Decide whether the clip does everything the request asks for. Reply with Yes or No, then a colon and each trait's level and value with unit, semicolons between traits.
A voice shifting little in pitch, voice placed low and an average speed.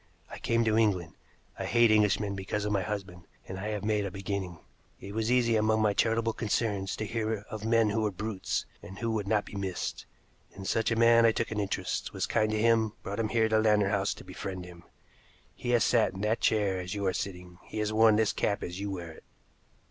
No: narrow, 2.3 semitones; low, 105 Hz; fast, 230 wpm